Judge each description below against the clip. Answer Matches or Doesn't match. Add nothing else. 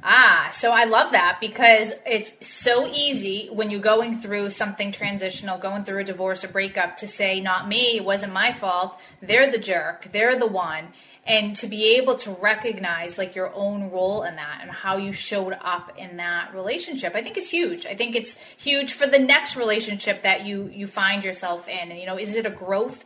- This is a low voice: Doesn't match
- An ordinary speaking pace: Doesn't match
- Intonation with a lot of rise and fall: Doesn't match